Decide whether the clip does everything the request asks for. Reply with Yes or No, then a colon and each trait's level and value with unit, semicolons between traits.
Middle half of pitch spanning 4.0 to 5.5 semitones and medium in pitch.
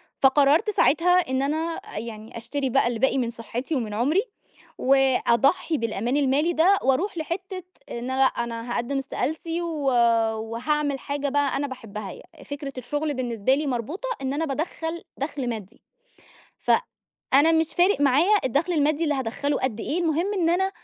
No: average, 4.5 semitones; very high, 280 Hz